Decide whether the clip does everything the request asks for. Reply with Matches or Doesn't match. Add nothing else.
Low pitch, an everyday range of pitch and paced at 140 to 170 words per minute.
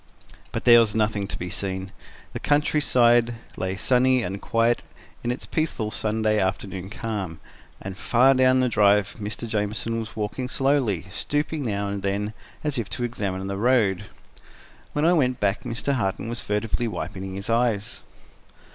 Matches